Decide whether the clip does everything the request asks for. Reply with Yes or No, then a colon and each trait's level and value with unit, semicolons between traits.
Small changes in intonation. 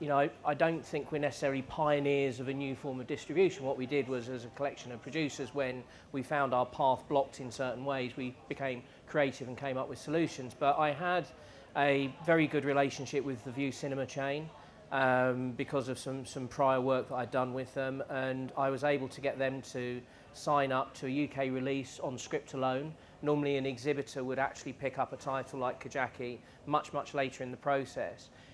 Yes: narrow, 1.6 semitones